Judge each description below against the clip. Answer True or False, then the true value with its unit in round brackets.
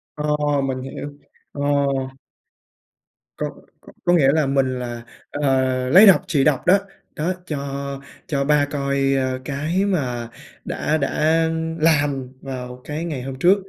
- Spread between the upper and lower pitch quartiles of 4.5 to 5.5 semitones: False (2.6 semitones)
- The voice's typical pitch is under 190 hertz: True (140 Hz)